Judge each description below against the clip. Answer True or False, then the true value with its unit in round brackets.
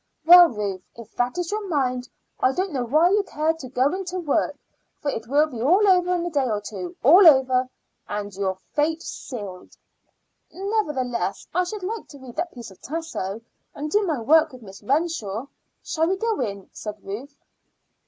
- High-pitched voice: True (285 Hz)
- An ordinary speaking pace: True (195 wpm)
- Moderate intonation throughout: False (7.2 semitones)